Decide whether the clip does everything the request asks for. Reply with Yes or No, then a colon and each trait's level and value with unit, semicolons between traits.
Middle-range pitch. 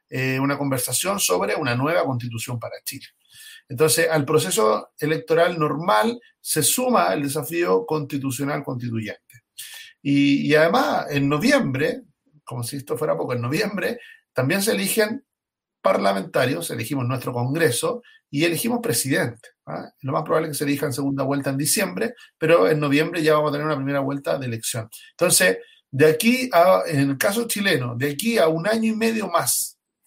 Yes: medium, 155 Hz